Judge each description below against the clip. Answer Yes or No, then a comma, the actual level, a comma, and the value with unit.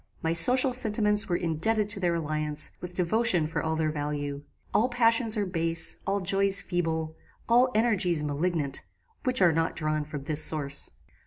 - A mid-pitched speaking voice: Yes, medium, 170 Hz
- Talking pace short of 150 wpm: No, average, 165 wpm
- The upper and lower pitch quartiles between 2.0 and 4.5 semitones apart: No, average, 5.2 semitones